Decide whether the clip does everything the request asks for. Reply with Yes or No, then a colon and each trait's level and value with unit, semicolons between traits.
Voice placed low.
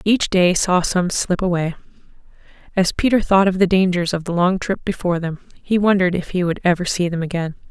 No: medium, 180 Hz